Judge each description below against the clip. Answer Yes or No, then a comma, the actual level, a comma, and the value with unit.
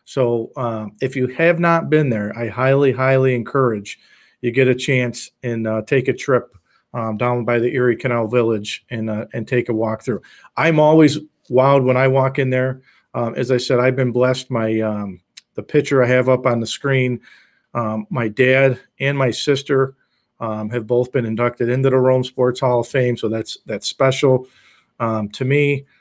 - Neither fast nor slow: Yes, average, 195 wpm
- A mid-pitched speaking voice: No, low, 125 Hz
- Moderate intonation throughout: No, narrow, 2.3 semitones